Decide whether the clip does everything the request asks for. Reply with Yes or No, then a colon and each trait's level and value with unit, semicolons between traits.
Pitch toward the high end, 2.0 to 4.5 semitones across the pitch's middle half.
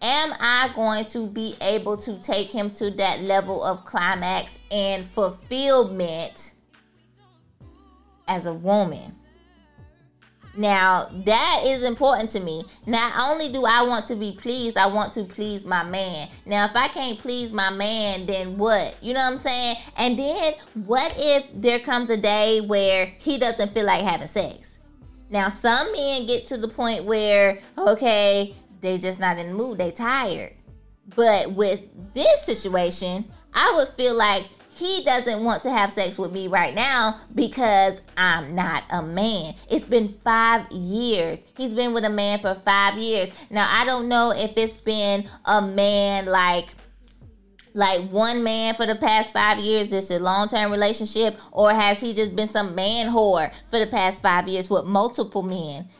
Yes: high, 210 Hz; average, 3.4 semitones